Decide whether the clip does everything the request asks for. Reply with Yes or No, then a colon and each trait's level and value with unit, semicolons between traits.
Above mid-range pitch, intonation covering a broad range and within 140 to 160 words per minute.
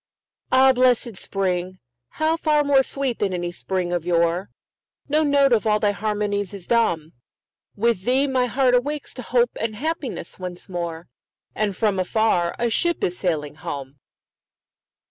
Yes: high, 210 Hz; wide, 6.3 semitones; average, 150 wpm